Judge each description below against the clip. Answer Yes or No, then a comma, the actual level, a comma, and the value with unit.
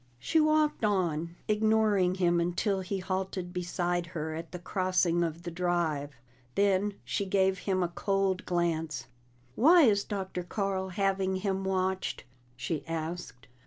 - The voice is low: No, medium, 185 Hz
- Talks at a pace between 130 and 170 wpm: Yes, average, 140 wpm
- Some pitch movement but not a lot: No, narrow, 2.3 semitones